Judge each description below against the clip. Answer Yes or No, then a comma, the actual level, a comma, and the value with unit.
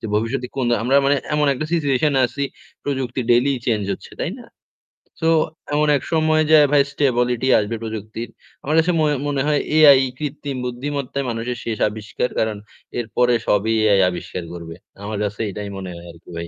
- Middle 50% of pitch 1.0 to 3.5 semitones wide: No, average, 4.8 semitones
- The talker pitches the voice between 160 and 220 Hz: No, low, 125 Hz